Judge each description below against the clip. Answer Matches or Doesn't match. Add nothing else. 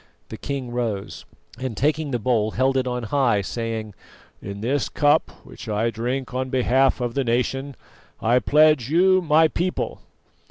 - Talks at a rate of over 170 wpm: Doesn't match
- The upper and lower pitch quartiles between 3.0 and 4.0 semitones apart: Matches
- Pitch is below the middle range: Matches